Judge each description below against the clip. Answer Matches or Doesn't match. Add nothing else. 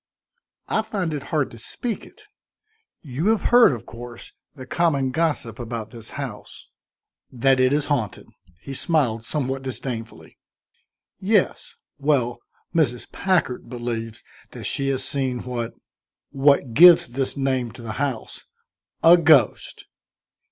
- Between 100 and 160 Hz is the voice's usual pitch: Matches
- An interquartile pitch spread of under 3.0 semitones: Doesn't match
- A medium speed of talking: Doesn't match